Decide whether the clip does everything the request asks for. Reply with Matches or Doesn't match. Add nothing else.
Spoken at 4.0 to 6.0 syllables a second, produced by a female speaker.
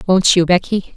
Matches